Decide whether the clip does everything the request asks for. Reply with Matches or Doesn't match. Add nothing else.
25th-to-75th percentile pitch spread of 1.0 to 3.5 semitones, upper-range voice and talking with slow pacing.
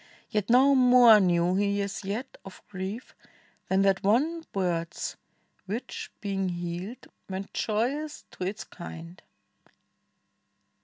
Doesn't match